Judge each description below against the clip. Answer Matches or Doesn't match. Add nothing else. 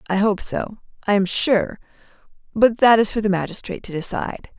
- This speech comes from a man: Doesn't match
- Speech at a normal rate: Matches